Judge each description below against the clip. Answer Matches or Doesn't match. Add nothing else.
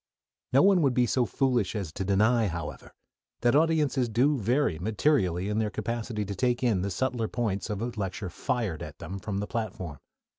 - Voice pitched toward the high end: Doesn't match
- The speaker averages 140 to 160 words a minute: Doesn't match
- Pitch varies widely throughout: Doesn't match